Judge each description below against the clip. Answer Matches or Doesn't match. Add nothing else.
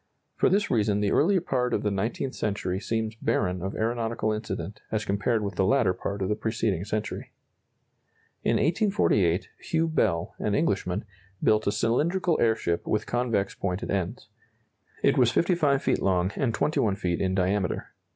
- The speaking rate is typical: Matches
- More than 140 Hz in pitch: Doesn't match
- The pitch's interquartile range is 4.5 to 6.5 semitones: Doesn't match